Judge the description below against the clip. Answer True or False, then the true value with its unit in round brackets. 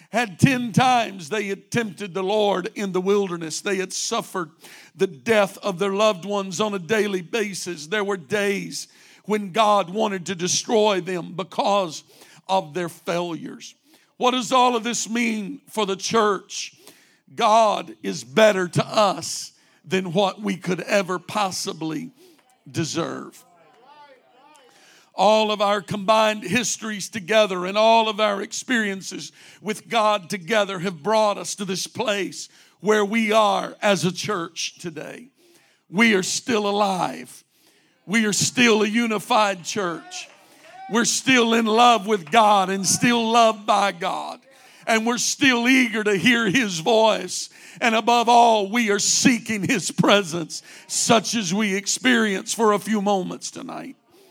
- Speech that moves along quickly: False (145 wpm)